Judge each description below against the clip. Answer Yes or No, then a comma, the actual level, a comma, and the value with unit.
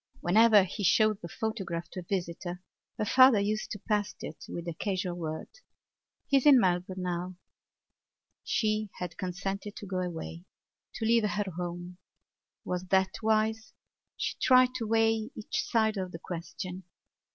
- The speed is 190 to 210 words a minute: No, average, 155 wpm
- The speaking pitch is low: No, high, 195 Hz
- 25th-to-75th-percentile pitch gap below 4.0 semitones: Yes, average, 3.5 semitones